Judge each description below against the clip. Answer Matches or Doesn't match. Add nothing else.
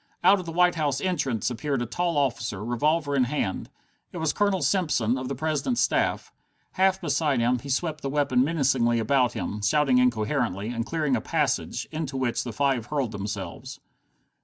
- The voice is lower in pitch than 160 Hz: Matches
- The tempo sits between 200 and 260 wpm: Doesn't match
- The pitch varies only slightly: Doesn't match